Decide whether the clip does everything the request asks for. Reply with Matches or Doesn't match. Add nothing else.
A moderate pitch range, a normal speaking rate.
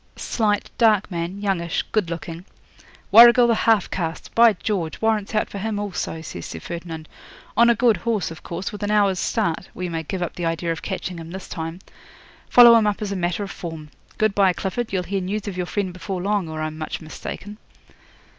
Doesn't match